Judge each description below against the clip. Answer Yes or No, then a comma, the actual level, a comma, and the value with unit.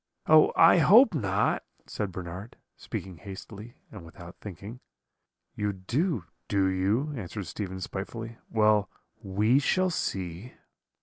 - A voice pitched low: Yes, low, 105 Hz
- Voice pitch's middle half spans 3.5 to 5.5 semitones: Yes, average, 4.3 semitones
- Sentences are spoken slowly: Yes, slow, 120 wpm